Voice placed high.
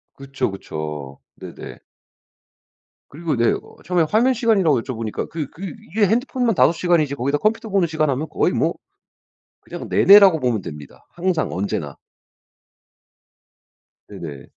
No: medium, 155 Hz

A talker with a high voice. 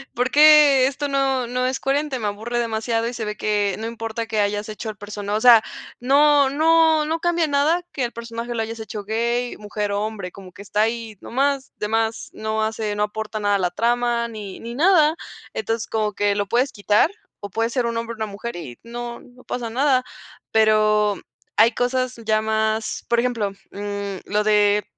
Yes: high, 225 Hz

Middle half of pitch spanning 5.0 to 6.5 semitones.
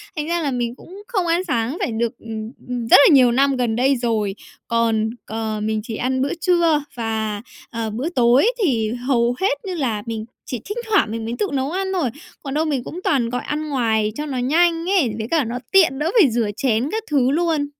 Yes: wide, 5.5 semitones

